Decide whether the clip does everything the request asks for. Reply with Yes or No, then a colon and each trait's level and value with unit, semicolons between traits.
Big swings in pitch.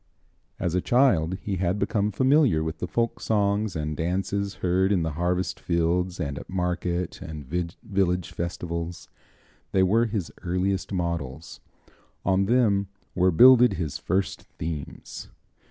No: average, 2.9 semitones